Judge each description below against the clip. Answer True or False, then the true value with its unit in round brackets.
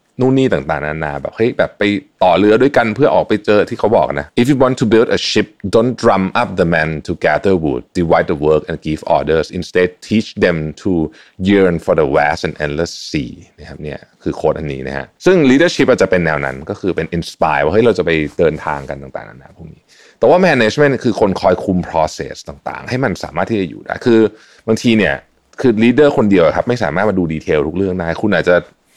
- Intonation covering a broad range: True (6.1 semitones)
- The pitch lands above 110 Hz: False (90 Hz)